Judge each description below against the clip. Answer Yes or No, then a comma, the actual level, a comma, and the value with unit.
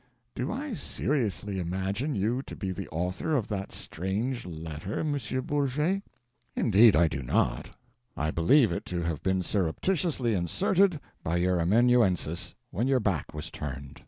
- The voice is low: Yes, low, 100 Hz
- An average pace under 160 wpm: Yes, average, 150 wpm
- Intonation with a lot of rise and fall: Yes, wide, 7.3 semitones